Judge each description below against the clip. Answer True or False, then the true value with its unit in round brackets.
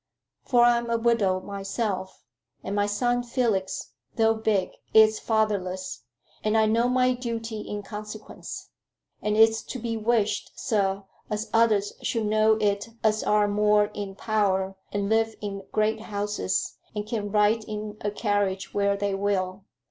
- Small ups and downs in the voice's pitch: True (1.7 semitones)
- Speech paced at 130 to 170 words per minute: True (150 wpm)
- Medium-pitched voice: False (210 Hz)